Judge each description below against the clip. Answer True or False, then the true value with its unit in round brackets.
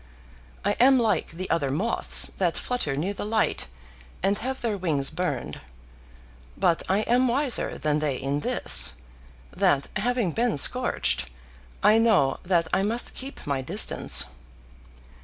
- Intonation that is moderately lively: False (7.7 semitones)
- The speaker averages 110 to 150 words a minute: True (140 wpm)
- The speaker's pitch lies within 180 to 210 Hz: True (190 Hz)